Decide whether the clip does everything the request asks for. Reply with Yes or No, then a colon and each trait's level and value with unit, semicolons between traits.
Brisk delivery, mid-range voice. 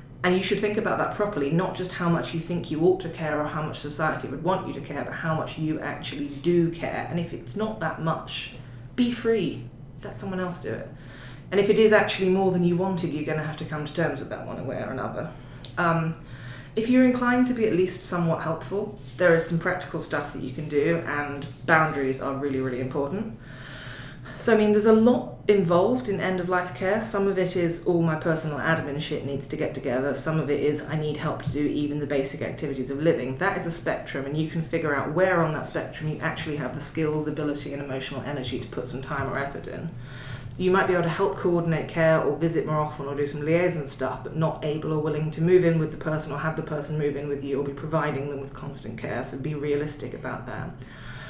Yes: fast, 245 wpm; medium, 155 Hz